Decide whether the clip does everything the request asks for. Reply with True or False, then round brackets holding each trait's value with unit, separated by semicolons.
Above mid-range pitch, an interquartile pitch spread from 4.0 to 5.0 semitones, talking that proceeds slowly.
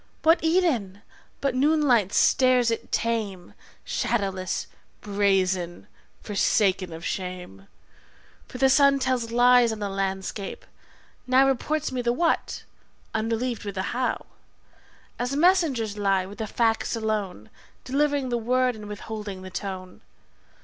True (225 Hz; 4.7 semitones; 130 wpm)